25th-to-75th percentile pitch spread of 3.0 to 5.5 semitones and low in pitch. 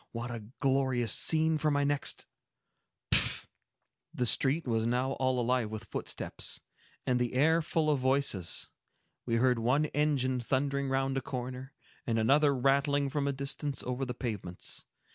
No: narrow, 2.4 semitones; low, 130 Hz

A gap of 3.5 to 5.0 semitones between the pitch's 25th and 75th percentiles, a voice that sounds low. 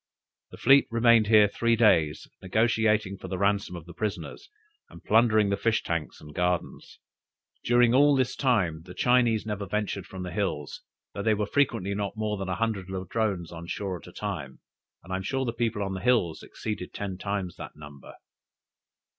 Yes: average, 3.8 semitones; low, 100 Hz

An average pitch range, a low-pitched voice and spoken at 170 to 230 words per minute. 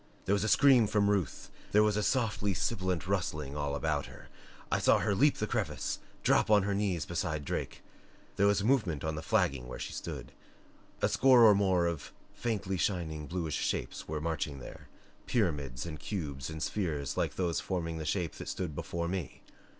Yes: average, 4.7 semitones; very low, 90 Hz; average, 185 wpm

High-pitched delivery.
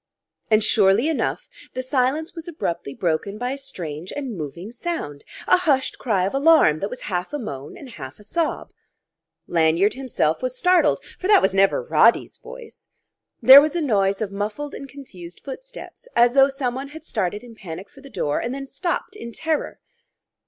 Yes: high, 245 Hz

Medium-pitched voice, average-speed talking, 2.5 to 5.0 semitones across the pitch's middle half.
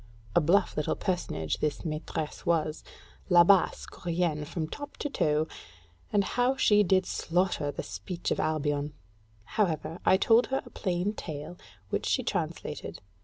Yes: medium, 170 Hz; average, 145 wpm; average, 4.0 semitones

